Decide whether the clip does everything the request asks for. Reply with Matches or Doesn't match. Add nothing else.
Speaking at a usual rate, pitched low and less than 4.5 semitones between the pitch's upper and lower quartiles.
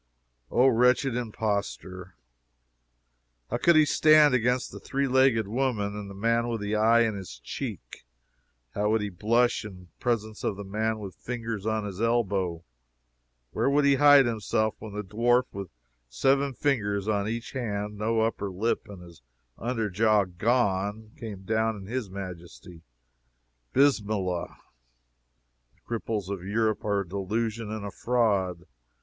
Matches